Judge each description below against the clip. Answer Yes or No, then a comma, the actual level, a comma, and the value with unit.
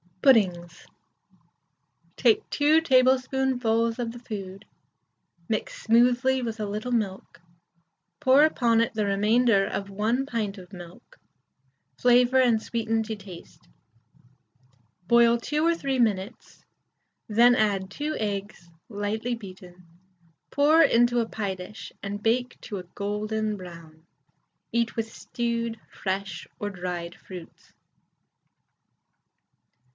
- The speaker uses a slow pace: Yes, slow, 115 wpm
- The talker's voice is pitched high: Yes, high, 220 Hz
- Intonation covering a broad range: No, average, 3.7 semitones